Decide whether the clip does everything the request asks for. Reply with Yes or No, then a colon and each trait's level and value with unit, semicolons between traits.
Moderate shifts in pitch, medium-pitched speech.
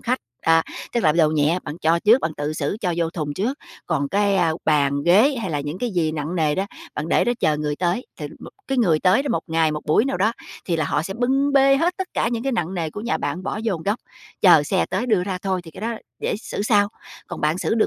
No: wide, 6.3 semitones; medium, 180 Hz